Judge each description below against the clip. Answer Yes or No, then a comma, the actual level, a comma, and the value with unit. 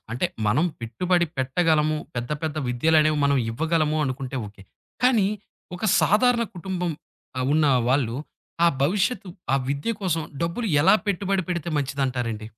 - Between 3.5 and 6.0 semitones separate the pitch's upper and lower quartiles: Yes, average, 5.3 semitones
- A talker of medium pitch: Yes, medium, 155 Hz